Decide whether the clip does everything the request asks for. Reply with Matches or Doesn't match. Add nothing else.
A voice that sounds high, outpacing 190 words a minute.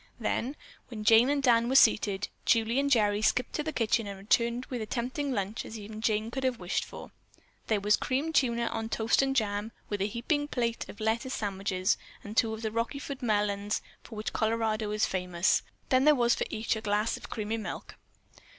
Matches